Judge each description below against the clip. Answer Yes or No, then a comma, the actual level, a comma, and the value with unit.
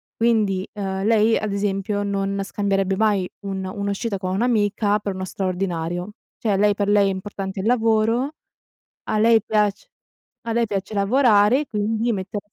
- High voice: Yes, high, 205 Hz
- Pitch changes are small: Yes, narrow, 2.1 semitones